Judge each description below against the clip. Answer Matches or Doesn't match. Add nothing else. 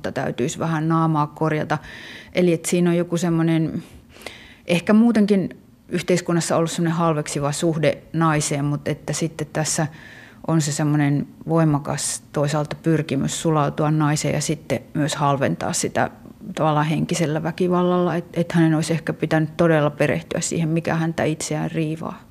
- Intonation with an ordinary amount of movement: Doesn't match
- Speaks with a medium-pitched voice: Matches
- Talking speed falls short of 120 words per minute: Doesn't match